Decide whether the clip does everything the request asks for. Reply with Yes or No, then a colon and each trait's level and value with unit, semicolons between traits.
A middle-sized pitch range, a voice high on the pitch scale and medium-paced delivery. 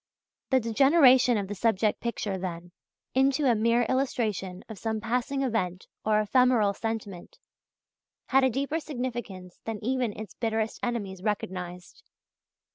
No: average, 4.1 semitones; high, 225 Hz; slow, 130 wpm